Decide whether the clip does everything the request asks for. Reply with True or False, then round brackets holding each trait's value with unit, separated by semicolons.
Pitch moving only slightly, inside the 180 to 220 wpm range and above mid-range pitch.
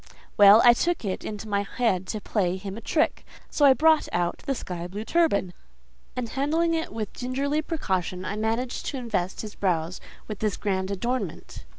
False (5.5 semitones; 185 wpm; 215 Hz)